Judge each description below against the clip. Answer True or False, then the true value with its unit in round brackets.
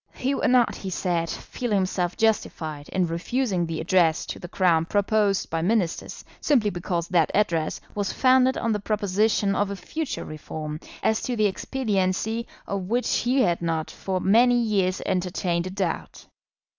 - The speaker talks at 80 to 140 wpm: False (165 wpm)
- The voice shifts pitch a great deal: False (4.2 semitones)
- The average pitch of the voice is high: True (195 Hz)